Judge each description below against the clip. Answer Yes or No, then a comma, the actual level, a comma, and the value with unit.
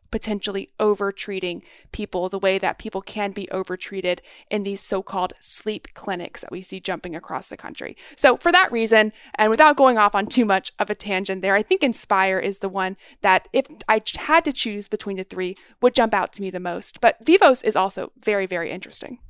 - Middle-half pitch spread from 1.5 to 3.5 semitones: Yes, narrow, 2.6 semitones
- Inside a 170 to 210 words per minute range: Yes, fast, 205 wpm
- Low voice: No, high, 200 Hz